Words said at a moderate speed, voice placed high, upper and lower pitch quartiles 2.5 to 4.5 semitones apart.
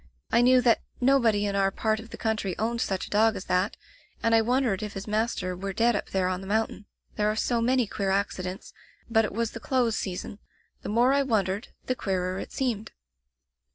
No: fast, 220 wpm; high, 215 Hz; average, 3.2 semitones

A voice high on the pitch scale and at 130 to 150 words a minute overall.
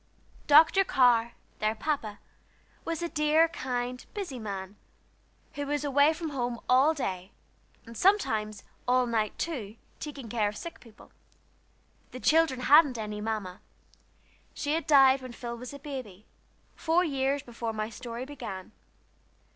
Yes: very high, 255 Hz; average, 140 wpm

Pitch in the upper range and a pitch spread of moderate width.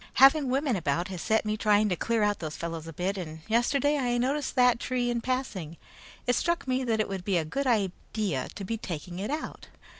No: high, 215 Hz; wide, 6.0 semitones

